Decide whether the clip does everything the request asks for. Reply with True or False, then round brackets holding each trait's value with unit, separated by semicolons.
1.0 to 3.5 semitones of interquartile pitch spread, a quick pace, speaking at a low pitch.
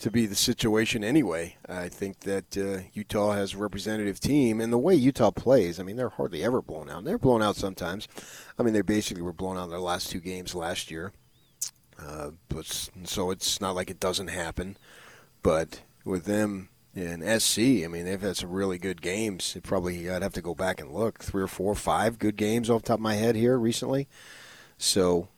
True (3.0 semitones; 220 wpm; 100 Hz)